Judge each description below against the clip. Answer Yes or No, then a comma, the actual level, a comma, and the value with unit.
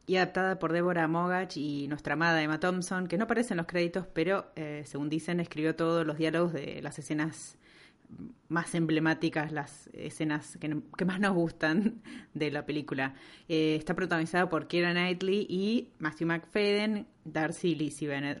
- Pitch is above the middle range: No, medium, 165 Hz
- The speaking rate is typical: Yes, average, 165 wpm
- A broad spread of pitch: No, average, 3.0 semitones